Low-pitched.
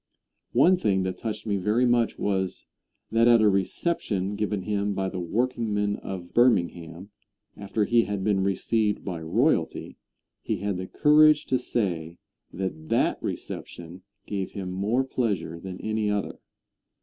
Yes: low, 100 Hz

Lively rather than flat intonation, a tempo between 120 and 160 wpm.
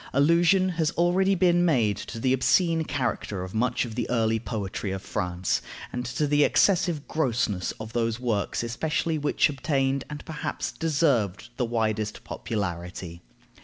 Yes: wide, 6.5 semitones; average, 150 wpm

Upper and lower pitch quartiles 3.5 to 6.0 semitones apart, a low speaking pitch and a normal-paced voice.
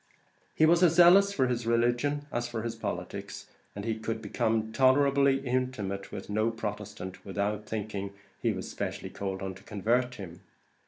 Yes: average, 4.0 semitones; low, 115 Hz; average, 165 wpm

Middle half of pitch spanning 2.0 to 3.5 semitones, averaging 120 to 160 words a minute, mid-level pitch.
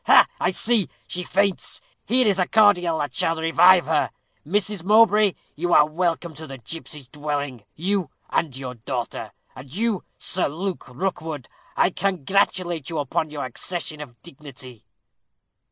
No: average, 4.7 semitones; average, 150 wpm; medium, 165 Hz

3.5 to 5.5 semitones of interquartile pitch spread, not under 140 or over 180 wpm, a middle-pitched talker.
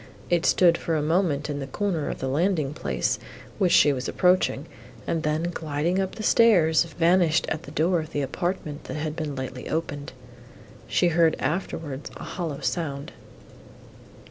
No: average, 3.1 semitones; average, 170 wpm; medium, 160 Hz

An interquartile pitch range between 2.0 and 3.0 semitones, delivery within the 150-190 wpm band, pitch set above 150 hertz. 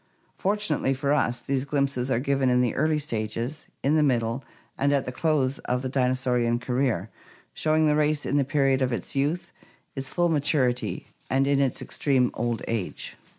No: average, 2.7 semitones; average, 180 wpm; low, 135 Hz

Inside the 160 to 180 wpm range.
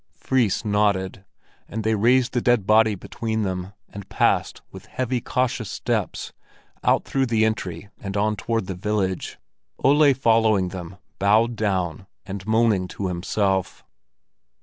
No: average, 140 wpm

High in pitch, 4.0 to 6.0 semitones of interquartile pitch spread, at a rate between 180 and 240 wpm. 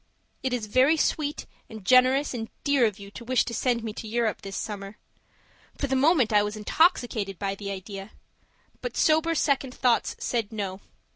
Yes: high, 235 Hz; average, 4.3 semitones; average, 185 wpm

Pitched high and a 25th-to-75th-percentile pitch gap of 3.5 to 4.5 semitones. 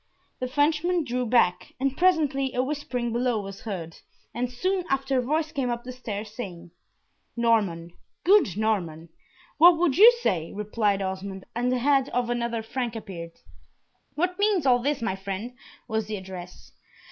No: high, 240 Hz; wide, 5.5 semitones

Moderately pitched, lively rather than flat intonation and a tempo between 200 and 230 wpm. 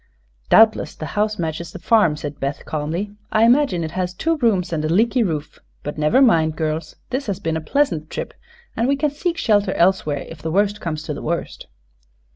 Yes: medium, 180 Hz; wide, 6.1 semitones; fast, 205 wpm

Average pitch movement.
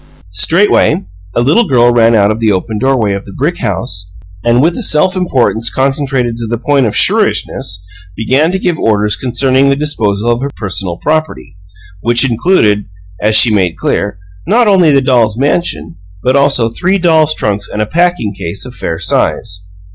No: wide, 5.9 semitones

